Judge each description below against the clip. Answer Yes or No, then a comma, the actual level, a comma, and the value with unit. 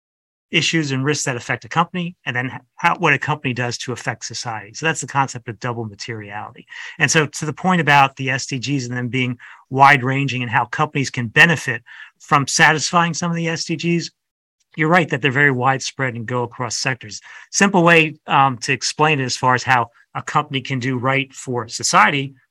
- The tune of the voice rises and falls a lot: No, average, 3.7 semitones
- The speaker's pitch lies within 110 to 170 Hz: Yes, low, 135 Hz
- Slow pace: No, average, 200 wpm